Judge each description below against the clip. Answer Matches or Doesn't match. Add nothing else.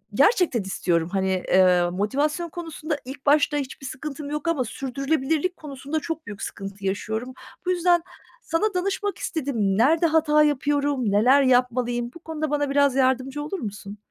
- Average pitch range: Matches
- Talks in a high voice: Matches